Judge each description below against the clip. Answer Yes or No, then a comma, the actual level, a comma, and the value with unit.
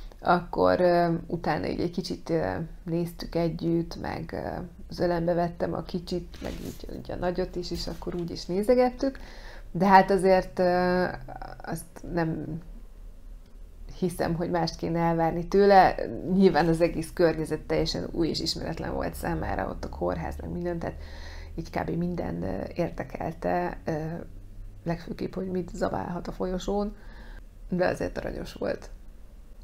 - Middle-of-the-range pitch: Yes, medium, 170 Hz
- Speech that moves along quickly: No, average, 130 wpm